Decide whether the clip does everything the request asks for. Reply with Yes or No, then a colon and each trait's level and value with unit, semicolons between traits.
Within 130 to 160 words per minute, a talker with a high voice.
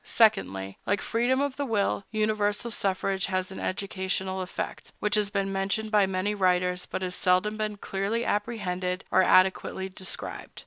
Yes: average, 155 wpm; high, 195 Hz